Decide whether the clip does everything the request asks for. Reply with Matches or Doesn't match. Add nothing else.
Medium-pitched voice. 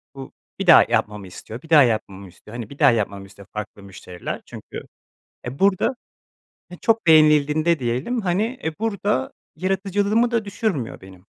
Matches